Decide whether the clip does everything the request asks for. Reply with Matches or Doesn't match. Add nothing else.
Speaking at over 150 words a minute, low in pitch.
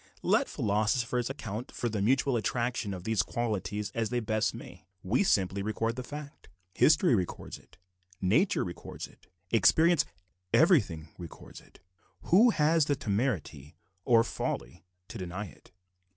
Doesn't match